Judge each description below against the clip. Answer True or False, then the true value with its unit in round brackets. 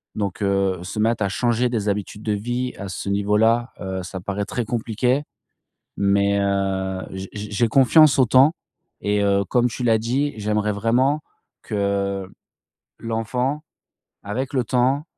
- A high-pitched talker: False (105 Hz)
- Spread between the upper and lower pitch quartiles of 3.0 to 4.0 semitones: True (3.6 semitones)